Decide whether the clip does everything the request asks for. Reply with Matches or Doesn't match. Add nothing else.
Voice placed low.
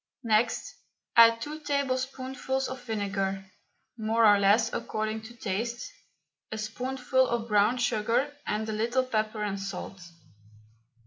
Doesn't match